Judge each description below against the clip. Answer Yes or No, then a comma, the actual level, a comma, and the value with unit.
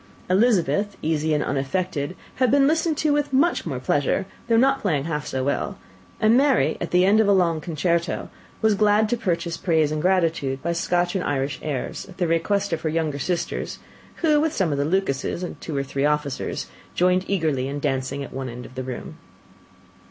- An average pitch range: No, wide, 5.8 semitones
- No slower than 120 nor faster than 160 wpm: No, average, 200 wpm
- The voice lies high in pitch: No, medium, 170 Hz